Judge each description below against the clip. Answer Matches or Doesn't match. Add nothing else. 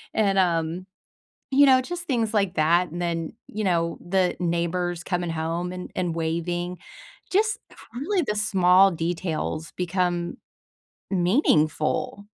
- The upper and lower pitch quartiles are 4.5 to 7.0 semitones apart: Doesn't match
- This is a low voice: Doesn't match